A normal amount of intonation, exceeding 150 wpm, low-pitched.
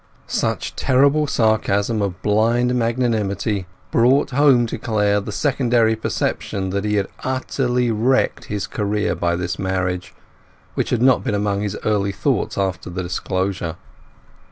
No: average, 3.9 semitones; average, 140 wpm; low, 105 Hz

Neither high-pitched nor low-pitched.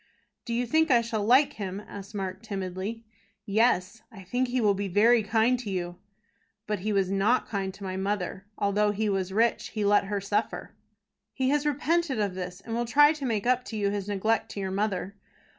No: high, 210 Hz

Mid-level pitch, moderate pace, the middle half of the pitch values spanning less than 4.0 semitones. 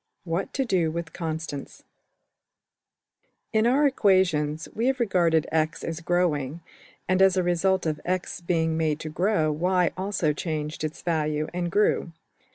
Yes: medium, 170 Hz; average, 150 wpm; average, 3.2 semitones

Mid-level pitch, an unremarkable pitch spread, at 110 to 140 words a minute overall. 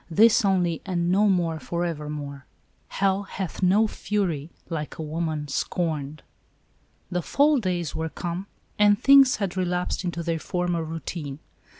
No: medium, 175 Hz; average, 3.3 semitones; average, 150 wpm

